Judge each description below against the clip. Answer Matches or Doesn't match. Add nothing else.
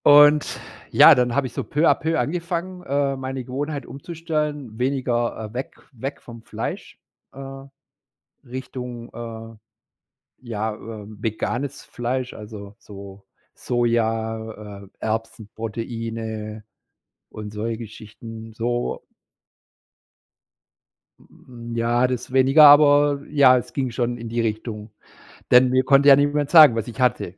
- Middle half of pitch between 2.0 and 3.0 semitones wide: Doesn't match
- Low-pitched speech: Matches